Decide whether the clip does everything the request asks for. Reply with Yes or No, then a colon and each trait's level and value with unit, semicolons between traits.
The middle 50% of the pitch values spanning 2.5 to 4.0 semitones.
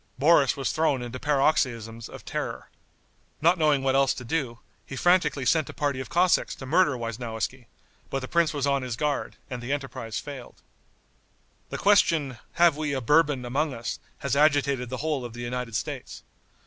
Yes: average, 3.5 semitones